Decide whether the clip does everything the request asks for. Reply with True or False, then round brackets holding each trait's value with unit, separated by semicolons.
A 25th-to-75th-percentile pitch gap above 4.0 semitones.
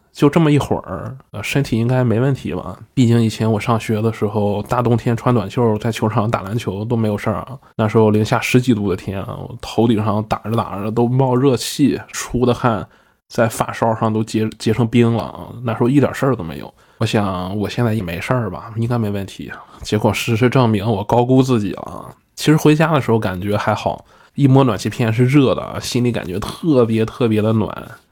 False (2.7 semitones)